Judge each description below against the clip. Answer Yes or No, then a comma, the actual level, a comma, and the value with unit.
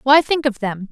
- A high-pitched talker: Yes, very high, 255 Hz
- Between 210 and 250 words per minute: No, fast, 265 wpm